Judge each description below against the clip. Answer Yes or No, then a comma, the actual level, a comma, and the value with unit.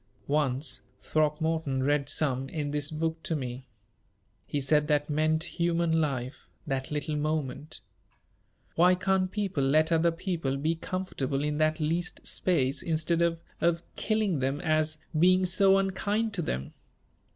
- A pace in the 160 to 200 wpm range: No, average, 140 wpm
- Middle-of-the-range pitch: Yes, medium, 155 Hz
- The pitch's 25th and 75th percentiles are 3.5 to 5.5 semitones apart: No, average, 2.9 semitones